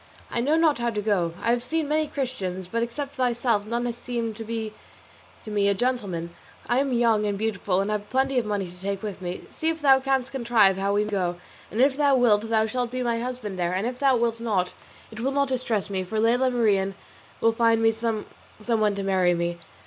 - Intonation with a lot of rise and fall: No, average, 3.8 semitones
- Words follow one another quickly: Yes, fast, 235 wpm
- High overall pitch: Yes, high, 225 Hz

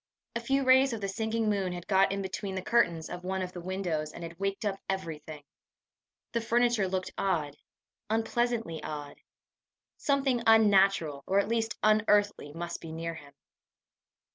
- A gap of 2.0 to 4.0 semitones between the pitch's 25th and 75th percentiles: No, average, 4.7 semitones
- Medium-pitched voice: No, high, 195 Hz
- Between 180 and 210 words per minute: No, average, 165 wpm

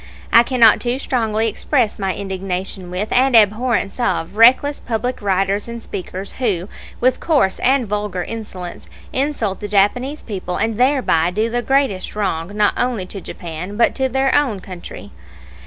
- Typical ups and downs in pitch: Yes, average, 4.5 semitones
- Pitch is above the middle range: Yes, high, 215 Hz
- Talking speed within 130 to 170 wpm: Yes, average, 155 wpm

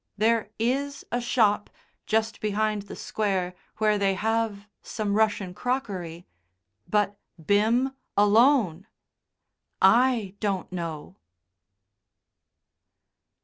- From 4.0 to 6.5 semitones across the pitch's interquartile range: No, narrow, 2.5 semitones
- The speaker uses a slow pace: Yes, slow, 90 wpm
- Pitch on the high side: Yes, high, 210 Hz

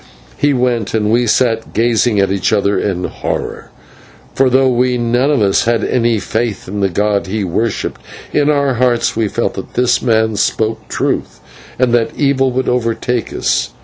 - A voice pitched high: No, low, 115 Hz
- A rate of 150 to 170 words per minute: No, average, 180 wpm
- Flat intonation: No, average, 3.0 semitones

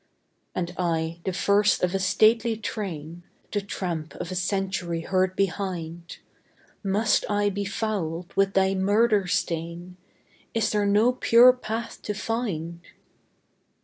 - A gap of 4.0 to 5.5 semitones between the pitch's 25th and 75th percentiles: No, average, 3.4 semitones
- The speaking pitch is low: No, high, 195 Hz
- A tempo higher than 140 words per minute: No, slow, 135 wpm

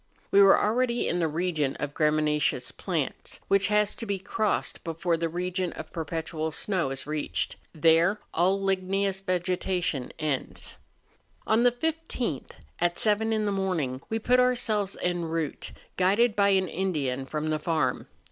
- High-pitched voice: No, medium, 180 Hz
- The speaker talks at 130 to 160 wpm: Yes, average, 155 wpm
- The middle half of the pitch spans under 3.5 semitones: No, average, 4.3 semitones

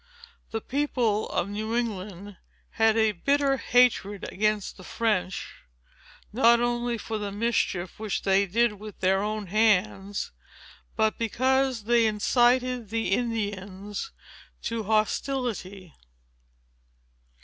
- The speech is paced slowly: Yes, slow, 110 wpm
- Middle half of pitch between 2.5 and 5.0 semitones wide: Yes, average, 2.9 semitones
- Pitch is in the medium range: No, high, 220 Hz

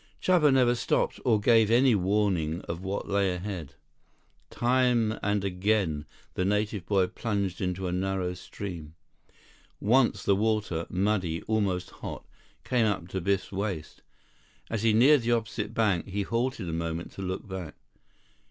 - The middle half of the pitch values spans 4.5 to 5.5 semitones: No, average, 3.5 semitones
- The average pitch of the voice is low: Yes, low, 100 Hz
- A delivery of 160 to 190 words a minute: No, average, 150 wpm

